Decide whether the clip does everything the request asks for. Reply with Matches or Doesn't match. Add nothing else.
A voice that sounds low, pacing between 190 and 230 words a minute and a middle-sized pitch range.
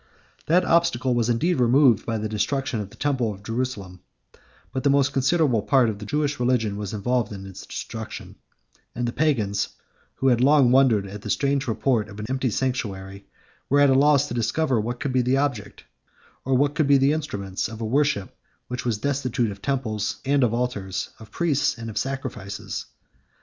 Matches